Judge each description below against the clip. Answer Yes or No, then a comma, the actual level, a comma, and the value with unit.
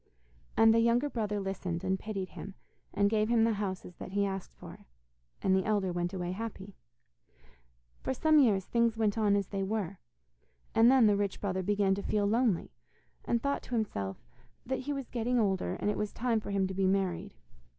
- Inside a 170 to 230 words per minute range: Yes, average, 200 wpm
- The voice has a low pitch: No, high, 205 Hz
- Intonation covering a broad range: No, average, 3.0 semitones